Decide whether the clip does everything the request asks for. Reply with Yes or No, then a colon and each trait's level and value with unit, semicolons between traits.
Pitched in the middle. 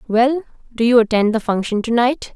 No: high, 235 Hz